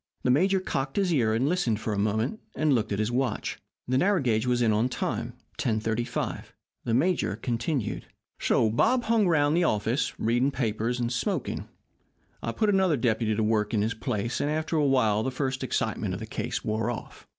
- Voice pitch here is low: Yes, low, 125 Hz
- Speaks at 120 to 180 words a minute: No, average, 200 wpm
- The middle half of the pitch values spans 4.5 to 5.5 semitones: Yes, average, 5.1 semitones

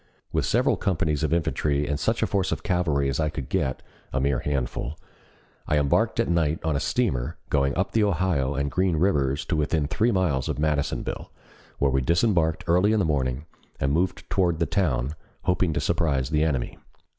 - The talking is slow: No, average, 190 wpm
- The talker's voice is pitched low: Yes, very low, 75 Hz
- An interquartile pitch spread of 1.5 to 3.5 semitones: No, average, 4.1 semitones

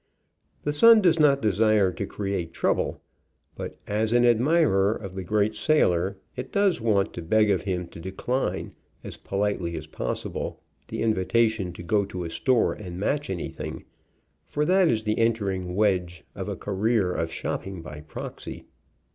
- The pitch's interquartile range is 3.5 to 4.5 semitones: Yes, average, 4.0 semitones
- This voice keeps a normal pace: Yes, average, 165 wpm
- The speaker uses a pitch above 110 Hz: No, low, 105 Hz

